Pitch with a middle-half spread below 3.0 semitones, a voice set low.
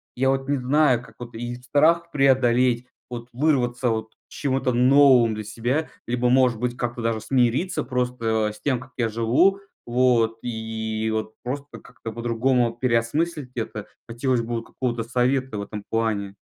Yes: narrow, 2.5 semitones; low, 120 Hz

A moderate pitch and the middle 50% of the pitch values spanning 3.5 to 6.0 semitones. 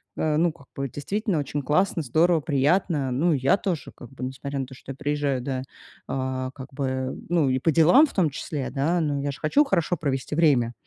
Yes: medium, 145 Hz; average, 4.0 semitones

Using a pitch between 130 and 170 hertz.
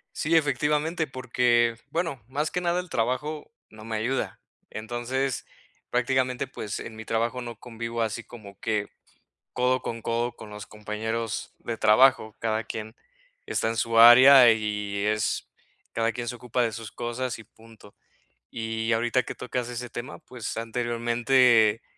No: low, 120 Hz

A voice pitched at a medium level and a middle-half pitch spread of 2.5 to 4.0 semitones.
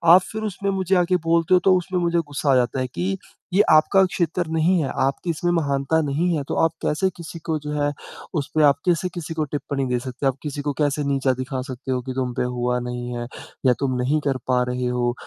No: medium, 145 Hz; average, 4.8 semitones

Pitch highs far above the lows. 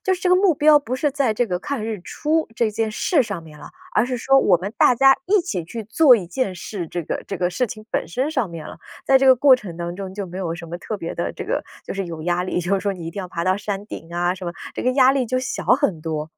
Yes: wide, 6.8 semitones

